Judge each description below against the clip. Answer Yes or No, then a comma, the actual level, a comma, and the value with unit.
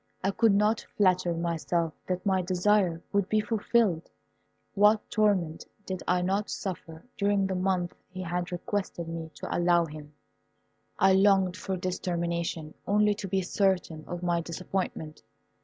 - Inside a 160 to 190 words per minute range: No, average, 150 wpm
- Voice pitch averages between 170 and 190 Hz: Yes, medium, 185 Hz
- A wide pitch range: No, average, 2.7 semitones